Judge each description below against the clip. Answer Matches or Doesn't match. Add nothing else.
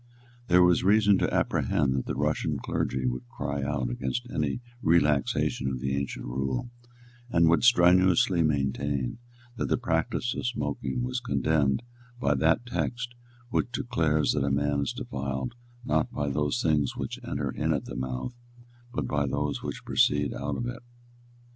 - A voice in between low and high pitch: Doesn't match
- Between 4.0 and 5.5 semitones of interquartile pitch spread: Matches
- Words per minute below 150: Doesn't match